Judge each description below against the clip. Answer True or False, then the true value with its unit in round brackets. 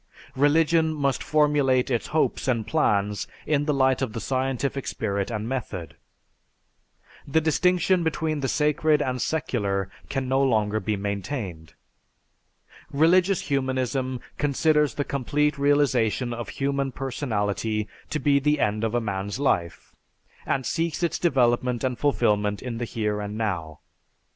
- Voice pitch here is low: True (130 Hz)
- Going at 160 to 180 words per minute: False (140 wpm)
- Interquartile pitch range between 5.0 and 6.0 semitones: True (5.4 semitones)